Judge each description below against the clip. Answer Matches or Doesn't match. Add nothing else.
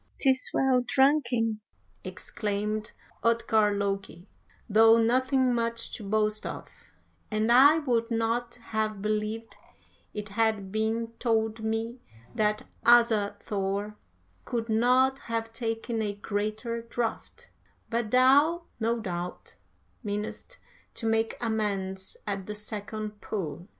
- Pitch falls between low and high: Doesn't match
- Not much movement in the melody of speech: Matches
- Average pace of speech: Doesn't match